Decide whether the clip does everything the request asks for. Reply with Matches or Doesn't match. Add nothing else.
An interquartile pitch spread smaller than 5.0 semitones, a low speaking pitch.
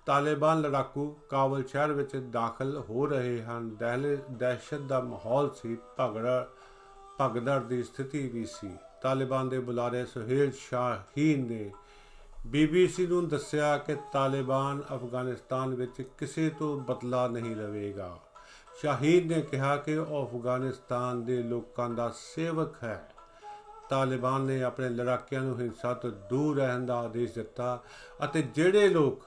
Matches